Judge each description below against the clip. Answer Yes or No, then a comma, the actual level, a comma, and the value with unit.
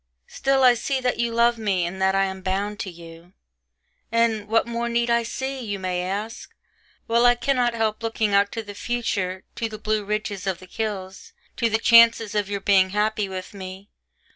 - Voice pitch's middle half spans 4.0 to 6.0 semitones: No, average, 3.4 semitones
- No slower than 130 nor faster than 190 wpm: No, average, 200 wpm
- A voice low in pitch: No, high, 215 Hz